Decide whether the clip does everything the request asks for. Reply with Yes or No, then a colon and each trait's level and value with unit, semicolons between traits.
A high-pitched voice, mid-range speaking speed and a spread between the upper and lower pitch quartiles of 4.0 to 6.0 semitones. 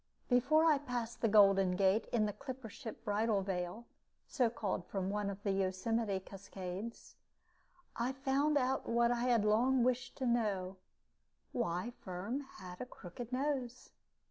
Yes: high, 225 Hz; average, 150 wpm; average, 4.3 semitones